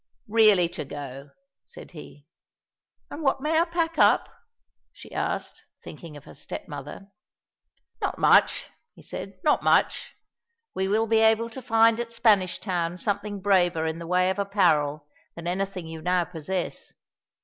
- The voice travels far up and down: No, average, 5.0 semitones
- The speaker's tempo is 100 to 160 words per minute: Yes, average, 155 wpm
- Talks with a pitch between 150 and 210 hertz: Yes, high, 190 Hz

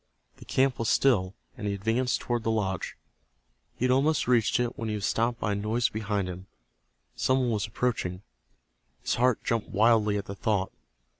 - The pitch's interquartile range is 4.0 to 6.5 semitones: No, average, 3.2 semitones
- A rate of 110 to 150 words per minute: No, average, 190 wpm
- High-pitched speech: No, low, 110 Hz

